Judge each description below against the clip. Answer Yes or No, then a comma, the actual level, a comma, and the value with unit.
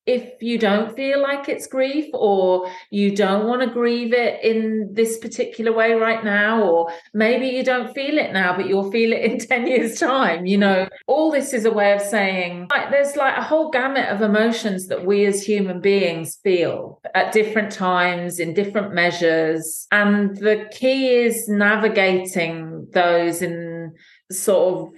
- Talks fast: No, average, 175 wpm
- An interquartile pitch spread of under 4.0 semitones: No, average, 4.4 semitones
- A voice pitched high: Yes, high, 210 Hz